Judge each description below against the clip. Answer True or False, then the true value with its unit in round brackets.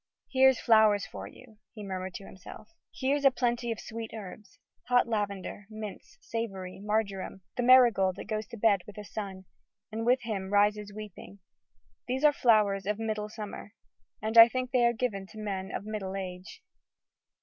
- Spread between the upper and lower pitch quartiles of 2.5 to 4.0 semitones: True (2.9 semitones)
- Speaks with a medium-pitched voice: False (215 Hz)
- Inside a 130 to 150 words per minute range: False (170 wpm)